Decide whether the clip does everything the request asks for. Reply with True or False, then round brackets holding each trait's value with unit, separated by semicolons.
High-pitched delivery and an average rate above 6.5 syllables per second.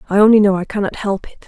True (200 Hz; 7.1 syllables/s)